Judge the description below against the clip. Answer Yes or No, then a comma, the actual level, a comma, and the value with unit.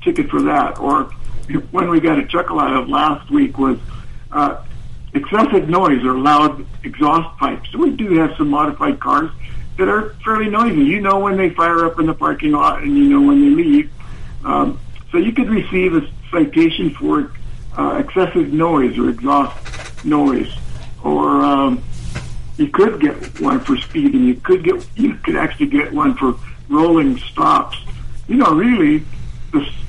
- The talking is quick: No, average, 175 wpm